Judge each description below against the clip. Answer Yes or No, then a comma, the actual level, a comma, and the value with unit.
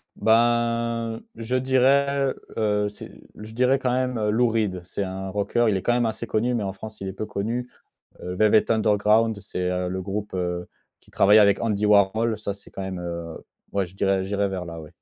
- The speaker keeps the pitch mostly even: No, average, 3.3 semitones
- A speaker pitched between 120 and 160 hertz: No, low, 105 Hz